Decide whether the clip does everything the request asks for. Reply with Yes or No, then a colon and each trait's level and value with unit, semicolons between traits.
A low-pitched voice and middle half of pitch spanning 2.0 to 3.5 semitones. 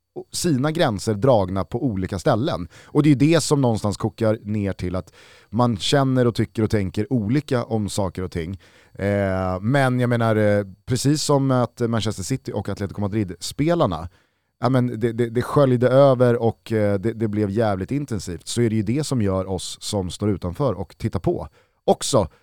No: low, 115 Hz; average, 4.1 semitones